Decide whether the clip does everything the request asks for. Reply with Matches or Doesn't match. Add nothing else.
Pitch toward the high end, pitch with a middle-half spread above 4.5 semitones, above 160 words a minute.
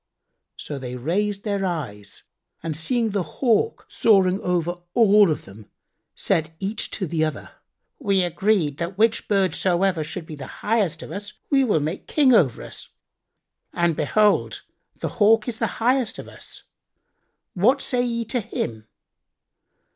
Doesn't match